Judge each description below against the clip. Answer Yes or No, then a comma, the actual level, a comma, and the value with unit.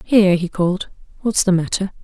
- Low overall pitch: No, high, 190 Hz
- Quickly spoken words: No, average, 175 wpm